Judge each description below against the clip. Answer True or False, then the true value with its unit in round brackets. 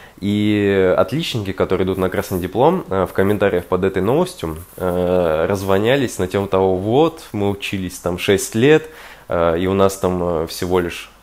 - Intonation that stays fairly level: True (2.0 semitones)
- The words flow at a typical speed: True (150 wpm)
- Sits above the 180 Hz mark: False (95 Hz)